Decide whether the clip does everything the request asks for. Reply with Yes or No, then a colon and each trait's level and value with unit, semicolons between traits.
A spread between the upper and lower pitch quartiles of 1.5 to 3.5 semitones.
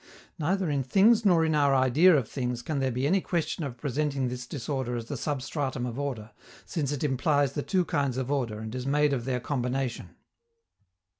Yes: average, 3.2 semitones